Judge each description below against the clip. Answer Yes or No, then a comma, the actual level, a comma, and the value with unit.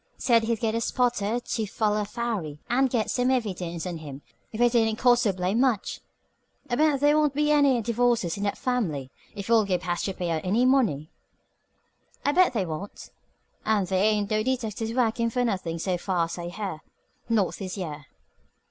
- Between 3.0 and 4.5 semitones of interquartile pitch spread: No, average, 4.9 semitones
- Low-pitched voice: No, high, 215 Hz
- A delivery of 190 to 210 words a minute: Yes, average, 195 wpm